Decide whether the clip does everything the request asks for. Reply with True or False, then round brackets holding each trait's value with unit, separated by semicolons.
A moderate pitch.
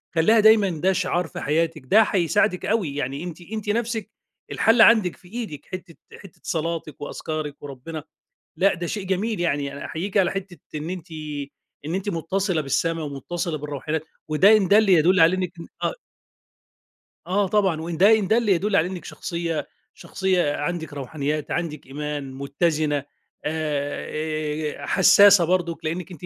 True (170 Hz)